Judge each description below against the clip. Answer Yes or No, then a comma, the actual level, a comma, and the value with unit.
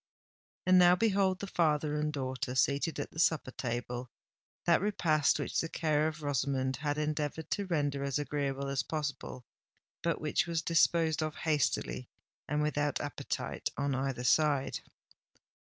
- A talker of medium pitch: Yes, medium, 150 Hz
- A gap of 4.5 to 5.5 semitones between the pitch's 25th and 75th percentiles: No, narrow, 2.6 semitones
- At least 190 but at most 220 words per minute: No, average, 145 wpm